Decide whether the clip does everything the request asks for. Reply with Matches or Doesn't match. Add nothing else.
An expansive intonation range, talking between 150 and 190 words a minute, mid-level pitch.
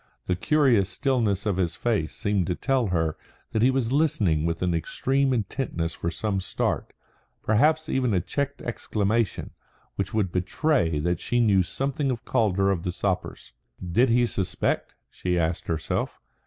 Doesn't match